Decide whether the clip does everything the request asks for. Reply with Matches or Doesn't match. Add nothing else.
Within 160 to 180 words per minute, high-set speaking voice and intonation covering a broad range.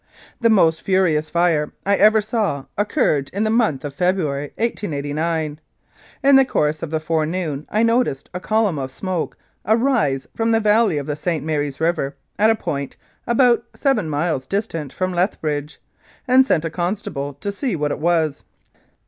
Doesn't match